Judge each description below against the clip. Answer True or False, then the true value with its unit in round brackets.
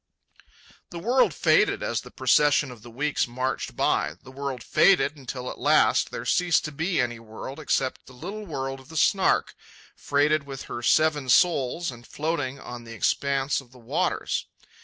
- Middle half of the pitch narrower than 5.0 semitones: True (3.8 semitones)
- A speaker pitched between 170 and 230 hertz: False (140 Hz)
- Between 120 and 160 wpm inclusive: False (175 wpm)